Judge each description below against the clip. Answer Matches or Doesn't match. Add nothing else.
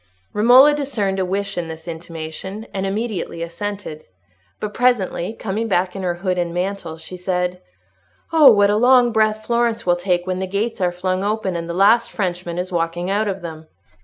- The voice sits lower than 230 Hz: Matches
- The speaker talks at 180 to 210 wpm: Matches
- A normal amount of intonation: Matches